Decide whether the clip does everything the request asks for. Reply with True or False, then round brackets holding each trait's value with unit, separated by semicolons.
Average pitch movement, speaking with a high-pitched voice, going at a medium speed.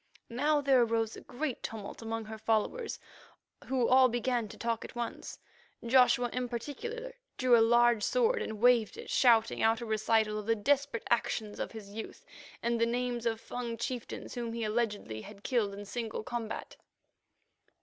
False (2.1 semitones; 235 Hz; 175 wpm)